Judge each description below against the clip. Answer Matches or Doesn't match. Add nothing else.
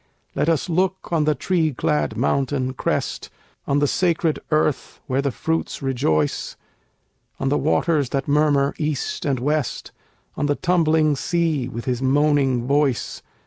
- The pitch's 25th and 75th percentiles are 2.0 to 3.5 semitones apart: Matches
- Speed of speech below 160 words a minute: Matches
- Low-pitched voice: Doesn't match